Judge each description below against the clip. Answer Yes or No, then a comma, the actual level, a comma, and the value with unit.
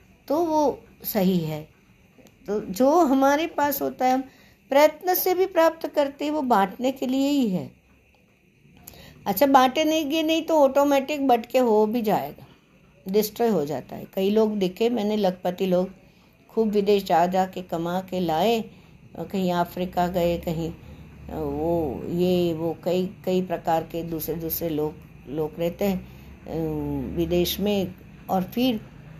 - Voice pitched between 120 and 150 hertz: No, high, 190 Hz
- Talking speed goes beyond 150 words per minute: No, average, 145 wpm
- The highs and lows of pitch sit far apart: Yes, wide, 7.2 semitones